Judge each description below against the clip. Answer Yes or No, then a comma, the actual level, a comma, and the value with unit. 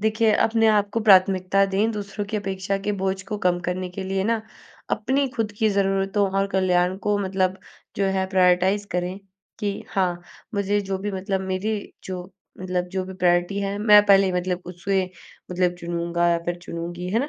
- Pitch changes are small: Yes, narrow, 2.0 semitones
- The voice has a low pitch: No, high, 195 Hz